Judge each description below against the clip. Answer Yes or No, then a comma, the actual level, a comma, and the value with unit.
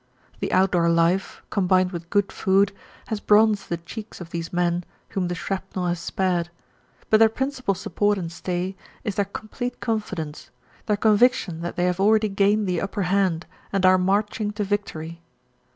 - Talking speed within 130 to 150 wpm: No, average, 170 wpm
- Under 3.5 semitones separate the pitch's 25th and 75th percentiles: Yes, average, 2.8 semitones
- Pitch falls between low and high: No, high, 195 Hz